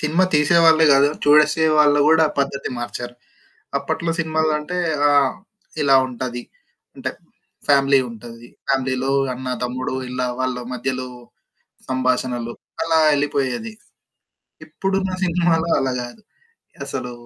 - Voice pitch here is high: No, medium, 140 Hz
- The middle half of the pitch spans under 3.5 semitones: No, average, 3.8 semitones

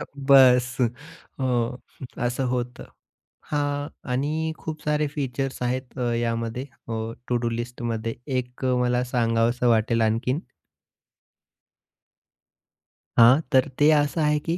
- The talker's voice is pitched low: Yes, low, 125 Hz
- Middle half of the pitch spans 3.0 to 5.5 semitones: Yes, average, 3.3 semitones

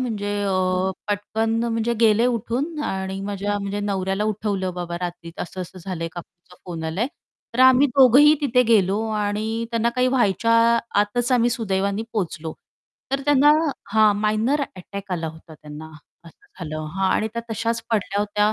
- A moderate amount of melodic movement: Yes, average, 3.8 semitones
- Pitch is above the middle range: Yes, high, 205 Hz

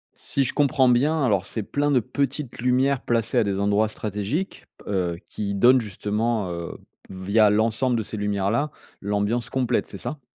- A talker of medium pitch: No, low, 115 Hz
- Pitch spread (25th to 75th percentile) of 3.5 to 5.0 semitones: Yes, average, 4.2 semitones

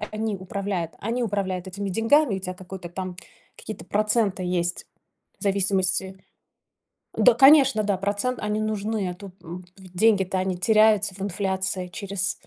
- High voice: Yes, high, 195 Hz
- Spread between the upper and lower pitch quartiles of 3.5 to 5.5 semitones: No, narrow, 2.5 semitones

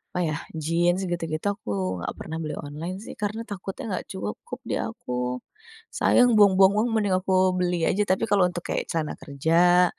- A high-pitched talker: No, medium, 175 Hz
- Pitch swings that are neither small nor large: Yes, average, 3.7 semitones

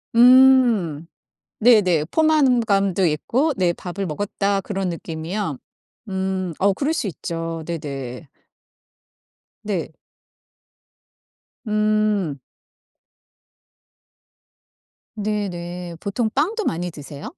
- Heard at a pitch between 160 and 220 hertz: Yes, high, 190 Hz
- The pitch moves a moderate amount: Yes, average, 4.4 semitones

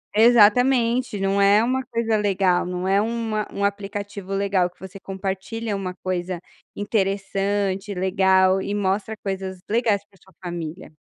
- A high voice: Yes, high, 200 Hz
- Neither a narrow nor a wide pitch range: No, narrow, 1.9 semitones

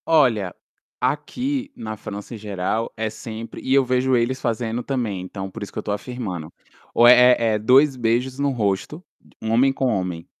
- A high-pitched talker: No, low, 120 Hz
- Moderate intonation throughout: Yes, average, 3.8 semitones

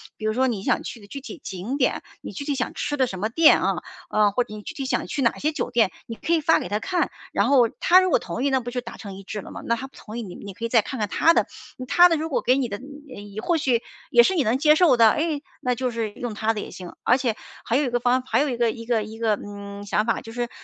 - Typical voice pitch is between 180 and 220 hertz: No, high, 240 Hz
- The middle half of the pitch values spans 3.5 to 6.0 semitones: Yes, average, 4.4 semitones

